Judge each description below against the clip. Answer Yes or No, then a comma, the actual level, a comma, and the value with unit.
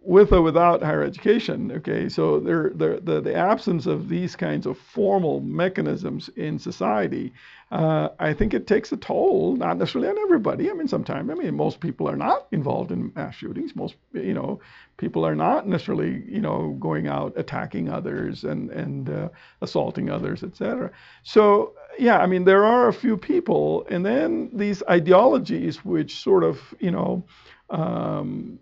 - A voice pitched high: Yes, high, 205 Hz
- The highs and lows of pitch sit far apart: Yes, wide, 7.6 semitones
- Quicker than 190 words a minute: No, average, 170 wpm